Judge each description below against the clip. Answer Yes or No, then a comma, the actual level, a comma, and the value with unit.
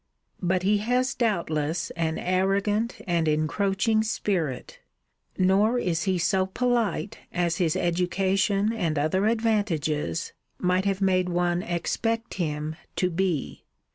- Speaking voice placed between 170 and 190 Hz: Yes, medium, 185 Hz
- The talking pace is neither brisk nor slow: No, slow, 120 wpm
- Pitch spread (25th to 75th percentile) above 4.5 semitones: No, average, 3.5 semitones